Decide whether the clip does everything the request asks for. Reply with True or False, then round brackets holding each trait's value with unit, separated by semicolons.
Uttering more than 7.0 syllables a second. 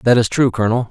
True (7.6 syllables/s)